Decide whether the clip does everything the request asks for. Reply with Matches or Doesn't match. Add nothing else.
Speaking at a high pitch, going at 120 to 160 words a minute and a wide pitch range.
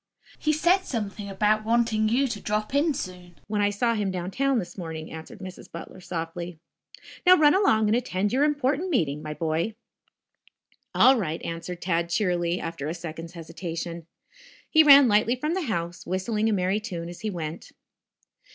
Doesn't match